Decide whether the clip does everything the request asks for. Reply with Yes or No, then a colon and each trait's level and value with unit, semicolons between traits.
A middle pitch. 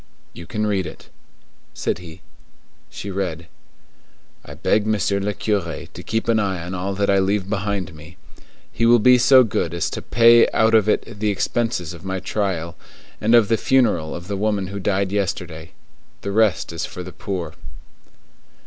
No: low, 100 Hz